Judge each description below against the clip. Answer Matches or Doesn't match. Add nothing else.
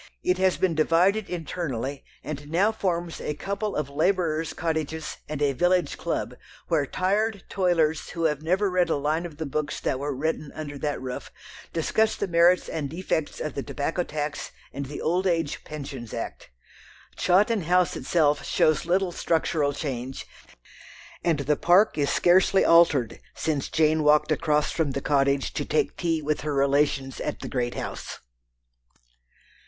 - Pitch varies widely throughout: Doesn't match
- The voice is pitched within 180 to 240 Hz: Doesn't match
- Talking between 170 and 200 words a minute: Doesn't match